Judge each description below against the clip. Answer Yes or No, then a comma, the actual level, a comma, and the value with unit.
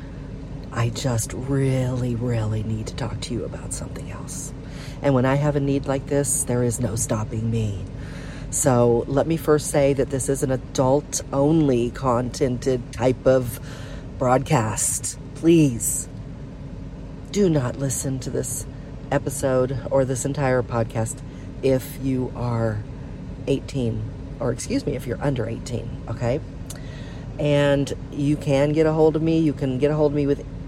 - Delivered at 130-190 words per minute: Yes, average, 155 wpm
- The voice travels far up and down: No, average, 2.8 semitones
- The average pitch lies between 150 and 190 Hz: No, low, 135 Hz